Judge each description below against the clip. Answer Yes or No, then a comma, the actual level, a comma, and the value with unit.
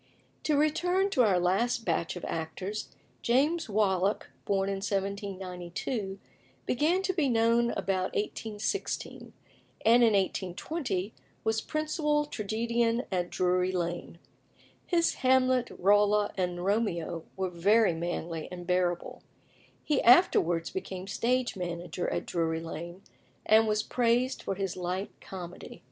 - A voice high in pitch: Yes, high, 200 Hz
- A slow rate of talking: Yes, slow, 125 wpm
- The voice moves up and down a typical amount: Yes, average, 4.8 semitones